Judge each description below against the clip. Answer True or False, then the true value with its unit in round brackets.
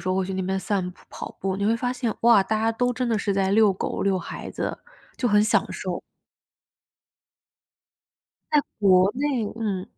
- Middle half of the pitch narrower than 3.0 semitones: False (3.3 semitones)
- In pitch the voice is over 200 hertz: True (210 Hz)